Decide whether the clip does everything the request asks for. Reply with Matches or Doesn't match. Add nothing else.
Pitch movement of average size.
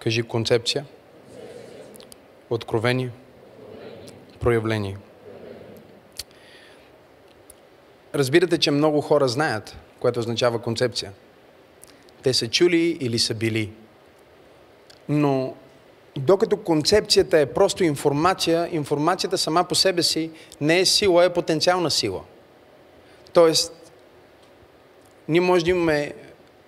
Doesn't match